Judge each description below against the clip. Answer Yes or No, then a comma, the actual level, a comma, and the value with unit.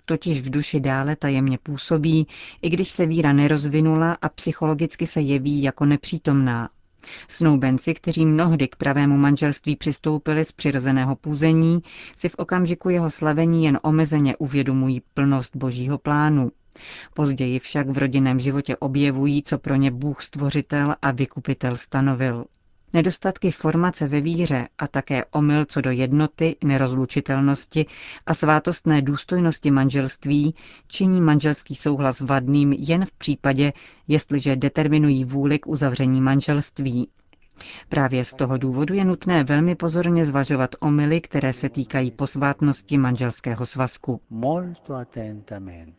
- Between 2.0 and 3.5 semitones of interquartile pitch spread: Yes, narrow, 2.6 semitones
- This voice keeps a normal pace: Yes, average, 125 wpm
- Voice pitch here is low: No, medium, 145 Hz